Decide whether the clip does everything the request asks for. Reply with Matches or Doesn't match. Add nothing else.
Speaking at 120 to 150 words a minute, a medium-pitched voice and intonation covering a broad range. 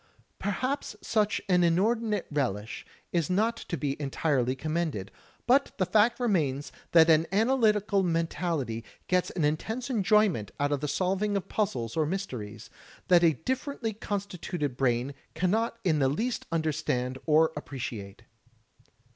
Matches